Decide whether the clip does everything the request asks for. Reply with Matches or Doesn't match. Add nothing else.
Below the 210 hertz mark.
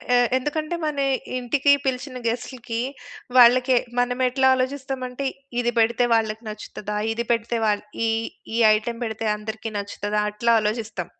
Doesn't match